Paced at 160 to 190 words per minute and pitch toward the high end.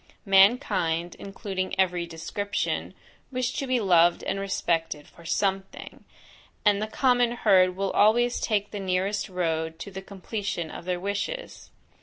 No: average, 140 wpm; high, 195 Hz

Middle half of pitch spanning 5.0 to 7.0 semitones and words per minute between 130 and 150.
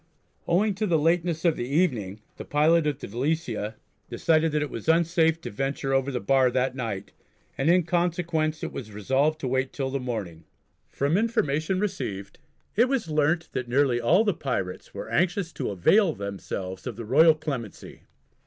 No: wide, 5.4 semitones; average, 180 wpm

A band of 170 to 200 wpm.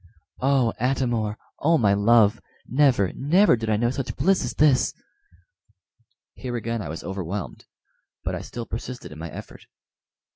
No: average, 155 wpm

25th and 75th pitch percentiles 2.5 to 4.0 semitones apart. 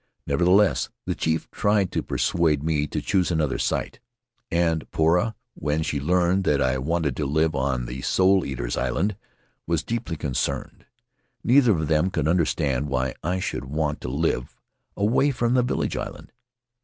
No: average, 4.6 semitones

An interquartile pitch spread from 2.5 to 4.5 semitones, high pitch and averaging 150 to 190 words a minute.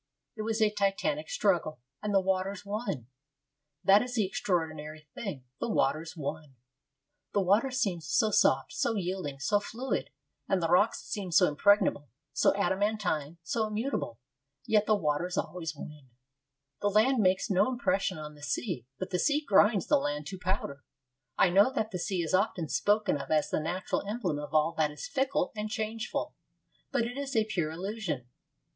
No: wide, 5.4 semitones; high, 195 Hz; average, 175 wpm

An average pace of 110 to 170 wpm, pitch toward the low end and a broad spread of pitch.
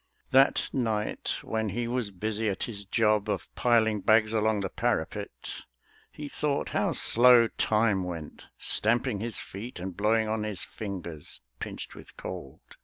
No: average, 150 wpm; low, 110 Hz; narrow, 2.5 semitones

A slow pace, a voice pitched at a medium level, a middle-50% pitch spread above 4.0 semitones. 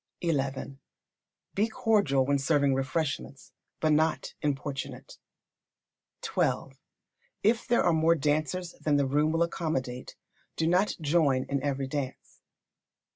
No: slow, 120 wpm; medium, 150 Hz; average, 3.5 semitones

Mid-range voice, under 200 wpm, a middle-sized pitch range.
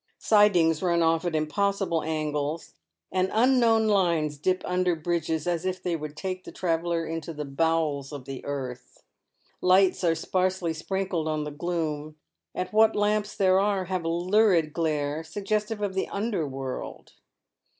Yes: medium, 170 Hz; average, 155 wpm; average, 3.7 semitones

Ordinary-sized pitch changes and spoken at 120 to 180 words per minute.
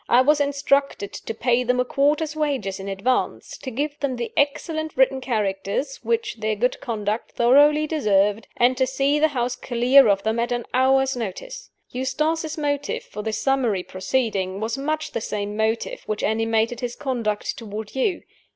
Yes: average, 4.6 semitones; average, 170 wpm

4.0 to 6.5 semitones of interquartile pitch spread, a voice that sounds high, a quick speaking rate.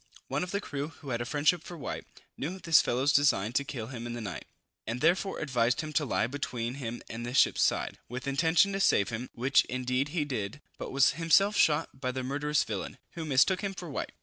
No: average, 4.5 semitones; medium, 140 Hz; fast, 230 wpm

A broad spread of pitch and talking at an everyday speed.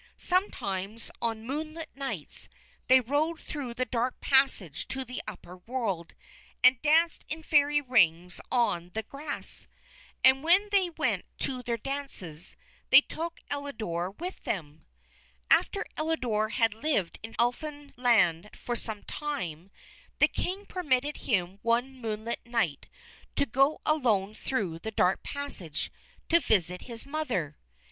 No: wide, 6.2 semitones; slow, 130 wpm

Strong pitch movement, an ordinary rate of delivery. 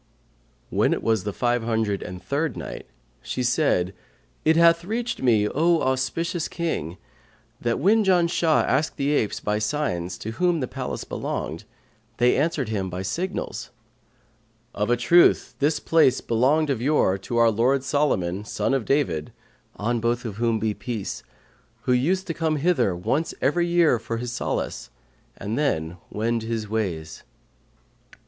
Yes: wide, 6.5 semitones; average, 155 wpm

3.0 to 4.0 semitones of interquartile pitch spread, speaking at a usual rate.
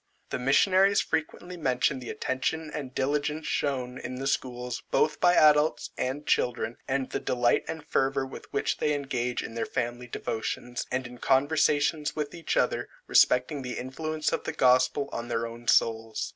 Yes: average, 3.3 semitones; average, 170 wpm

